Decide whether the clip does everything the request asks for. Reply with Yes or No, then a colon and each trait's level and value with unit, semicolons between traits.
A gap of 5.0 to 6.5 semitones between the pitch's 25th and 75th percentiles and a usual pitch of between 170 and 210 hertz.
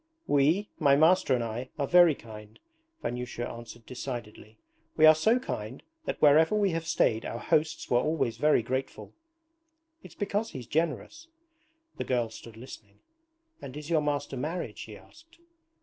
No: wide, 5.5 semitones; medium, 140 Hz